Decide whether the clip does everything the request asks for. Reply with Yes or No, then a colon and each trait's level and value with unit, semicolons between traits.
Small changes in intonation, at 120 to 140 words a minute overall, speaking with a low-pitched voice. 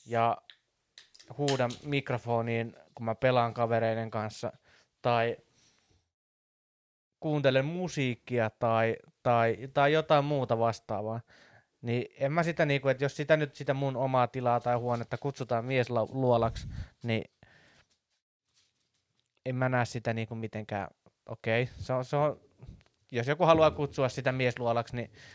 No: average, 3.0 semitones; average, 125 wpm; low, 120 Hz